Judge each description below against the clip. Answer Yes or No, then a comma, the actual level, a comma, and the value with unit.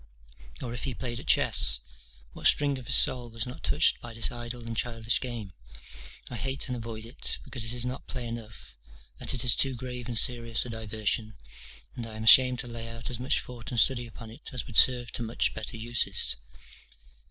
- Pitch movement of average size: No, narrow, 1.7 semitones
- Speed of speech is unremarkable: No, fast, 210 wpm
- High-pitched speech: No, low, 120 Hz